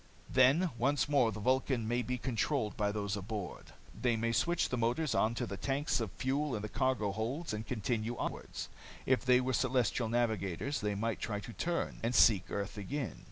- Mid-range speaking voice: No, low, 120 Hz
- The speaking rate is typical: Yes, average, 190 wpm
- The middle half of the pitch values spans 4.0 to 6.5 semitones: No, average, 3.6 semitones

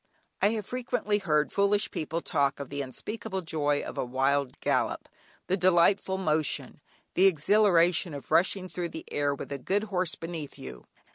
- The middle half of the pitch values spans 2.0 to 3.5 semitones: No, average, 5.2 semitones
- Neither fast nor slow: Yes, average, 165 wpm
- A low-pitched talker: No, medium, 170 Hz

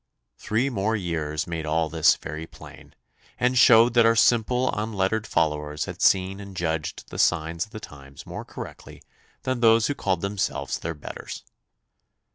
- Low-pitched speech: Yes, very low, 95 Hz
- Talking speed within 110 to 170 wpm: Yes, average, 160 wpm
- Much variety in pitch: Yes, wide, 5.9 semitones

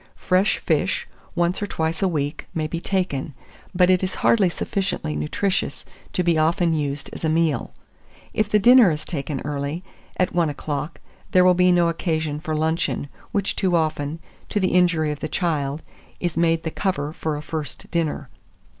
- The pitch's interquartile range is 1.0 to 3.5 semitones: Yes, average, 3.2 semitones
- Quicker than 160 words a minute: Yes, average, 180 wpm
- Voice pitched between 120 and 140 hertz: No, medium, 165 Hz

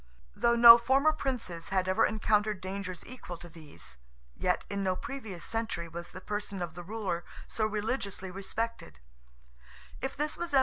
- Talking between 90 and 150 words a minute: Yes, slow, 135 wpm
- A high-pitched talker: Yes, high, 195 Hz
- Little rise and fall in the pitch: No, average, 4.5 semitones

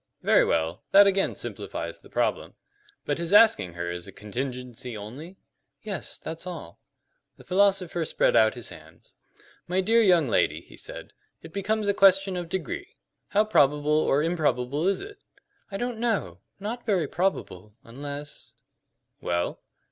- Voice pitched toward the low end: No, medium, 165 Hz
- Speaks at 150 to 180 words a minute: Yes, average, 155 wpm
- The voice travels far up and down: Yes, wide, 8.0 semitones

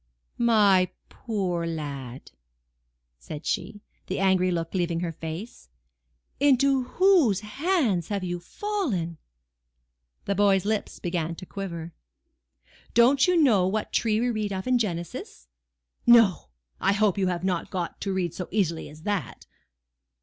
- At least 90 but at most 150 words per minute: Yes, slow, 135 wpm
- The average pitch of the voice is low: No, high, 190 Hz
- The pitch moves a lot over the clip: No, average, 4.6 semitones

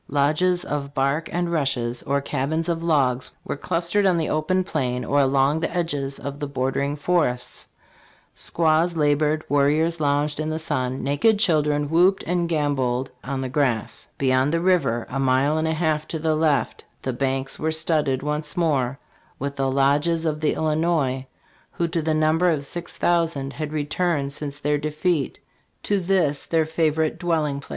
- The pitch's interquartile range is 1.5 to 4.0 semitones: Yes, average, 2.9 semitones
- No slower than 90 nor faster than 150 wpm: No, average, 170 wpm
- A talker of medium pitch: Yes, medium, 150 Hz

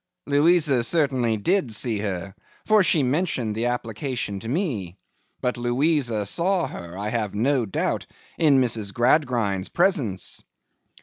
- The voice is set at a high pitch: No, low, 120 Hz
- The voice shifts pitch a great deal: Yes, wide, 5.9 semitones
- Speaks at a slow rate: Yes, slow, 130 wpm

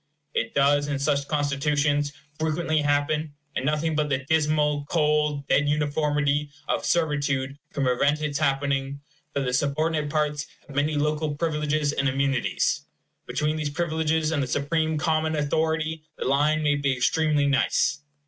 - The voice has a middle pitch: Yes, medium, 150 Hz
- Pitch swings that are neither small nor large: No, narrow, 1.5 semitones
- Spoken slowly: No, average, 150 wpm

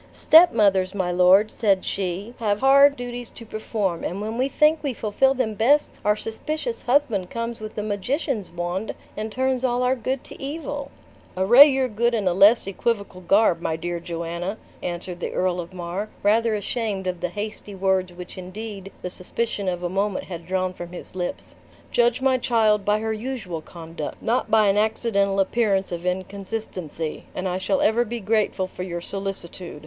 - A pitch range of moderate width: Yes, average, 4.2 semitones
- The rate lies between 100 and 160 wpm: No, average, 180 wpm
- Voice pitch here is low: No, high, 205 Hz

